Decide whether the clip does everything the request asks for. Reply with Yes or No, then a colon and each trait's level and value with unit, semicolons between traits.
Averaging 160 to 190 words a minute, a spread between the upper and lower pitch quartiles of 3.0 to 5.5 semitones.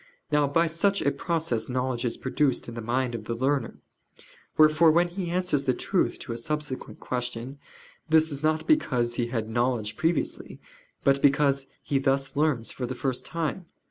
Yes: average, 175 wpm; average, 4.2 semitones